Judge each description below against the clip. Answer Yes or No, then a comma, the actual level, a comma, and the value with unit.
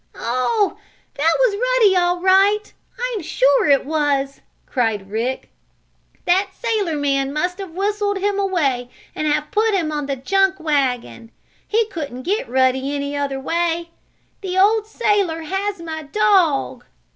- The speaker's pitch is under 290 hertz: No, very high, 335 Hz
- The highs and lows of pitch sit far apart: Yes, wide, 6.3 semitones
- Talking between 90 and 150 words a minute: Yes, average, 145 wpm